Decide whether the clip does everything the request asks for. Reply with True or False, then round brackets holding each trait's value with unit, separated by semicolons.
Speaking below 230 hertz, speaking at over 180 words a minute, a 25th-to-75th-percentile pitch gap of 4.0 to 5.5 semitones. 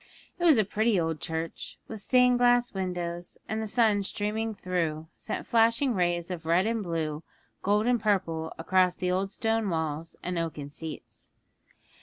False (185 Hz; 165 wpm; 4.9 semitones)